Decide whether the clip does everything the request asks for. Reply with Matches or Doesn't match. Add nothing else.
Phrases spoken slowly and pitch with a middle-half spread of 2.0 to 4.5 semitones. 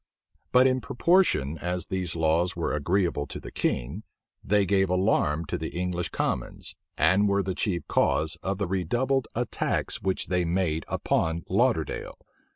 Doesn't match